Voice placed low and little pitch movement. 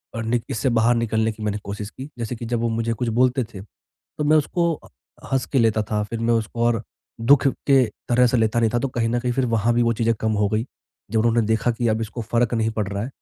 Yes: low, 115 Hz; narrow, 1.5 semitones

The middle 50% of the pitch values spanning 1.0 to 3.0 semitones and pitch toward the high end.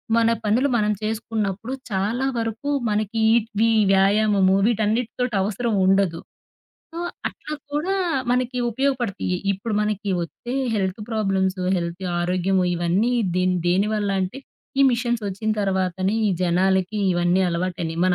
No: average, 3.4 semitones; high, 205 Hz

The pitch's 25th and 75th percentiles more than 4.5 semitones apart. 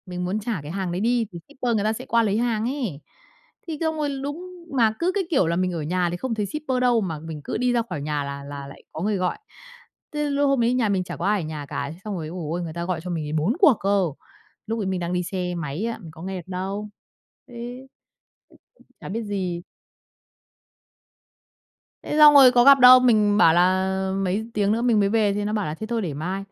Yes: average, 5.1 semitones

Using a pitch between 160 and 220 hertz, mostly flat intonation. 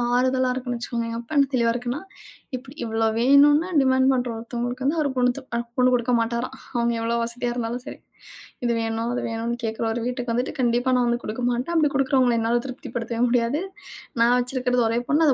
No: high, 245 Hz; narrow, 1.7 semitones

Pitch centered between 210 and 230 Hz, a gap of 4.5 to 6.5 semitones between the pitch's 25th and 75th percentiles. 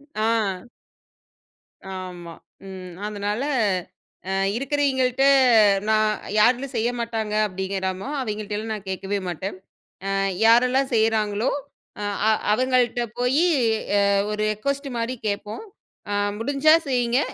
No: high, 220 Hz; average, 3.8 semitones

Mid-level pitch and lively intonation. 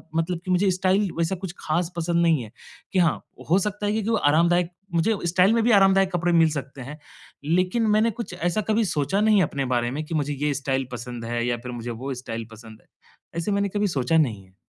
Yes: medium, 165 Hz; wide, 6.2 semitones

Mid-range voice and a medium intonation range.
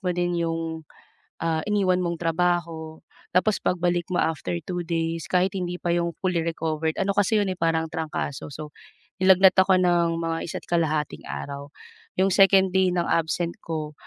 No: medium, 170 Hz; narrow, 2.0 semitones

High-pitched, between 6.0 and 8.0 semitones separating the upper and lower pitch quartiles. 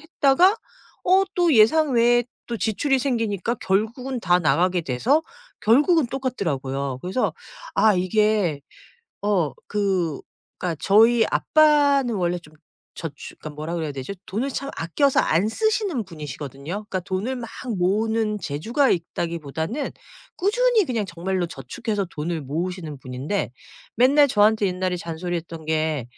Yes: high, 200 Hz; wide, 7.1 semitones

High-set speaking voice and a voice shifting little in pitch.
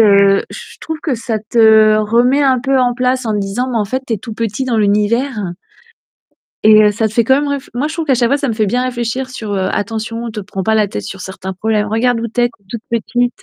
No: high, 230 Hz; average, 3.0 semitones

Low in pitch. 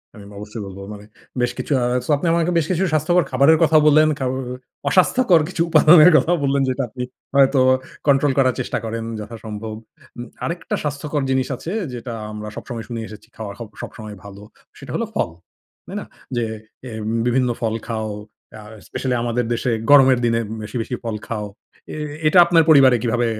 Yes: low, 125 Hz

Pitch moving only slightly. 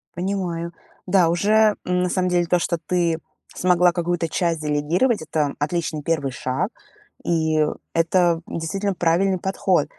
Yes: narrow, 2.1 semitones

